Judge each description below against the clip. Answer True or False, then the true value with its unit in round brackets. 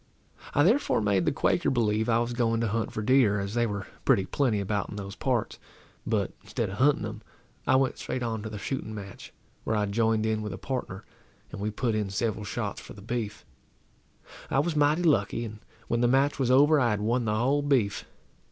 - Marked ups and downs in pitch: False (3.7 semitones)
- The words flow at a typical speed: False (215 wpm)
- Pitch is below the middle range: True (115 Hz)